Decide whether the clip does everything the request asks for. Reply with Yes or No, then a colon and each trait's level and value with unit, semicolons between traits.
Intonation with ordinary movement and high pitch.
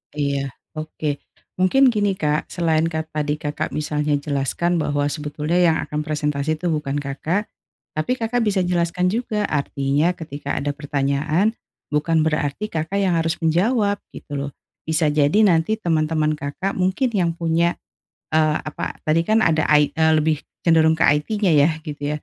No: average, 3.1 semitones; medium, 160 Hz